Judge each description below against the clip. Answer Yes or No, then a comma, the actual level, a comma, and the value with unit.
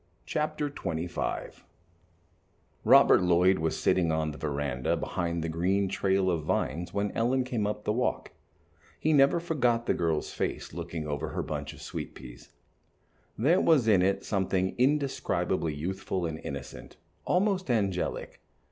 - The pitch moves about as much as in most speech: No, wide, 7.1 semitones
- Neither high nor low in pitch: No, very low, 95 Hz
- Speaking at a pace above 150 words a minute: No, average, 145 wpm